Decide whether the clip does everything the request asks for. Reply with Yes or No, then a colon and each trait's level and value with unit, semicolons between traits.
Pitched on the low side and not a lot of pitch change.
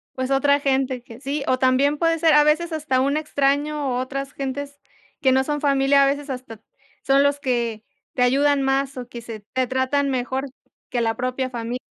No: very high, 270 Hz; narrow, 1.9 semitones